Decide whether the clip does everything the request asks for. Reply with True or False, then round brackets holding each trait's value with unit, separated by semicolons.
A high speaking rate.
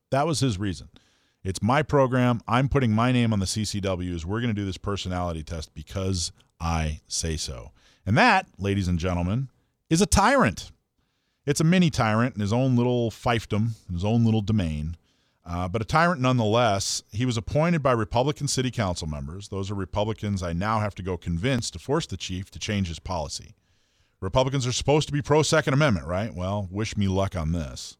False (195 wpm)